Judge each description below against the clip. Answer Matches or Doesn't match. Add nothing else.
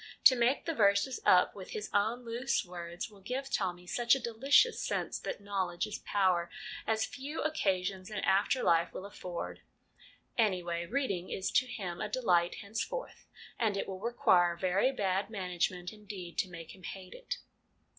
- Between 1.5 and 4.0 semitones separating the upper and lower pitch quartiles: Doesn't match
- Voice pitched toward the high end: Matches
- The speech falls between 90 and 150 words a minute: Doesn't match